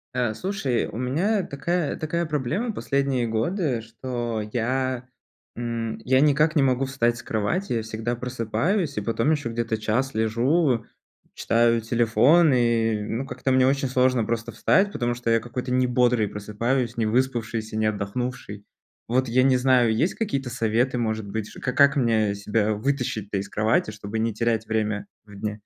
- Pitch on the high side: No, low, 120 Hz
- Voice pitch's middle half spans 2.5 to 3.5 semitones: Yes, average, 3.2 semitones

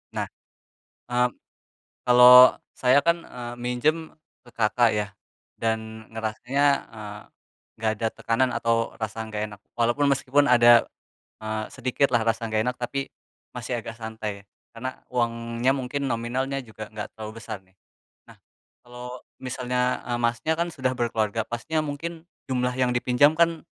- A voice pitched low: Yes, low, 120 Hz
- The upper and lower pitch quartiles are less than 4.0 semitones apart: Yes, narrow, 2.4 semitones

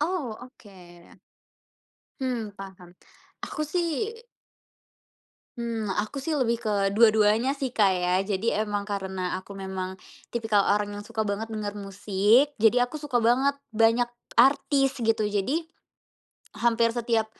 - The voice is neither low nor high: No, high, 220 Hz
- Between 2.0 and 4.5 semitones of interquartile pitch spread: Yes, average, 3.3 semitones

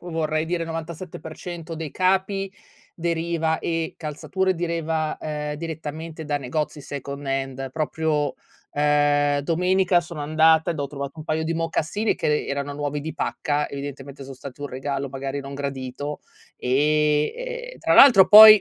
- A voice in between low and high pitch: Yes, medium, 155 Hz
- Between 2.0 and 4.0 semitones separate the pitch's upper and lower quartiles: Yes, average, 2.8 semitones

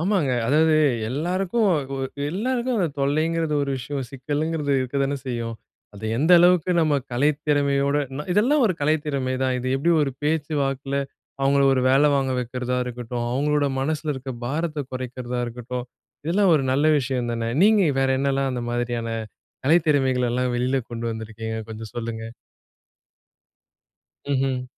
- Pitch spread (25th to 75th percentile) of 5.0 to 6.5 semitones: No, average, 3.5 semitones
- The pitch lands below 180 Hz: Yes, low, 135 Hz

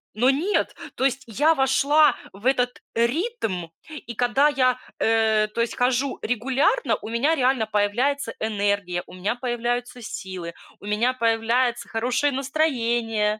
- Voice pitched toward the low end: No, high, 245 Hz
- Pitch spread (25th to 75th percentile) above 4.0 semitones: No, average, 3.5 semitones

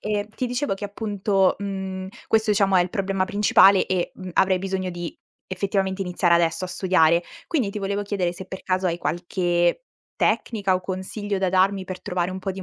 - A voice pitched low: No, high, 190 Hz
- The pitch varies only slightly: Yes, narrow, 1.6 semitones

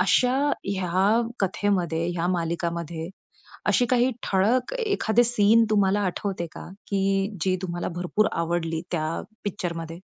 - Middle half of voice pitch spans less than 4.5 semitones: Yes, average, 3.7 semitones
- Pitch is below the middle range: No, high, 190 Hz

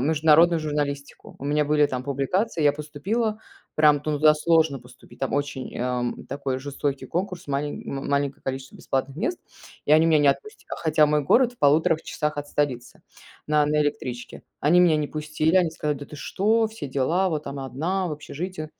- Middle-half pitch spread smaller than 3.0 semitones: Yes, narrow, 2.5 semitones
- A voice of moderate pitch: Yes, medium, 150 Hz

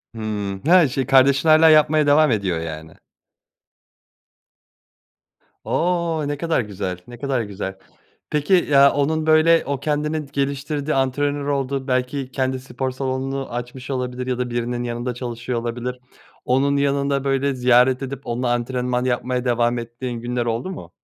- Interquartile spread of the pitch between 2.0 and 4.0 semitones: Yes, average, 2.7 semitones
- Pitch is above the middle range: No, low, 130 Hz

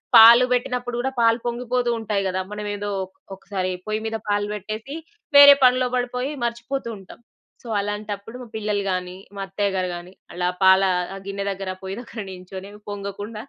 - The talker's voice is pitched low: No, high, 210 Hz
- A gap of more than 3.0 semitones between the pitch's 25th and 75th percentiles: Yes, average, 3.5 semitones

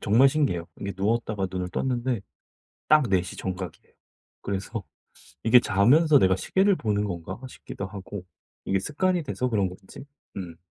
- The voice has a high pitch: No, low, 100 Hz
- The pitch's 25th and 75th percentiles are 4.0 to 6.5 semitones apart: Yes, wide, 5.6 semitones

